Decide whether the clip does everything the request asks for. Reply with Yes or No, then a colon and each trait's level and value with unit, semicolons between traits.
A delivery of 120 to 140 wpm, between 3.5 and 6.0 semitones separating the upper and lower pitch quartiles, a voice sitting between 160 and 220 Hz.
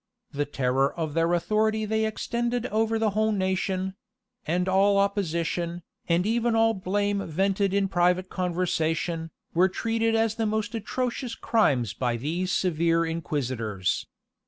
Yes: slow, 135 wpm; average, 4.7 semitones; high, 190 Hz